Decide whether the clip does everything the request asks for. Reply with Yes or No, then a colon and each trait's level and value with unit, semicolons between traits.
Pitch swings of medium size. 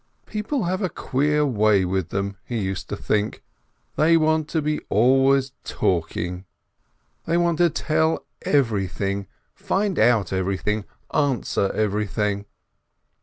No: wide, 8.0 semitones